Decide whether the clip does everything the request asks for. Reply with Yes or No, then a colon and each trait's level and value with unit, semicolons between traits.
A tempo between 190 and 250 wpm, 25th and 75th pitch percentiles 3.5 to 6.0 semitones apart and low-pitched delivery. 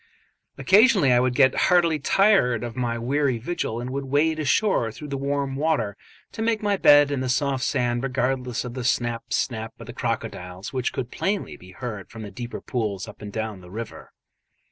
Yes: average, 195 wpm; average, 3.9 semitones; low, 125 Hz